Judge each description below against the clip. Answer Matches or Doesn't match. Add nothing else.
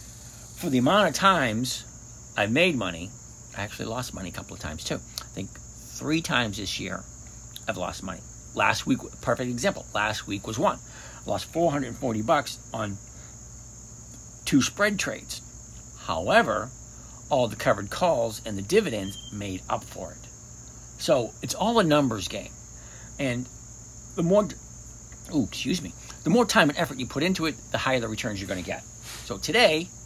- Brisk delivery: Doesn't match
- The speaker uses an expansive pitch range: Matches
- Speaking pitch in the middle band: Doesn't match